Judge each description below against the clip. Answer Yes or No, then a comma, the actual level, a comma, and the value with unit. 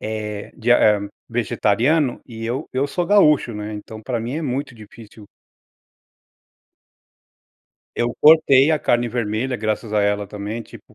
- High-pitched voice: No, low, 115 Hz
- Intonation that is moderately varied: Yes, average, 3.6 semitones